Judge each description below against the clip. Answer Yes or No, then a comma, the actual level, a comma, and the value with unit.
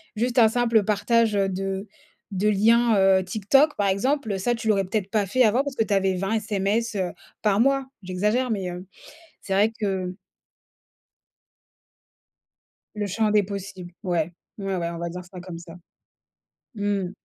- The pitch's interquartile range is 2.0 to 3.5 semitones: Yes, average, 3.0 semitones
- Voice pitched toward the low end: No, high, 200 Hz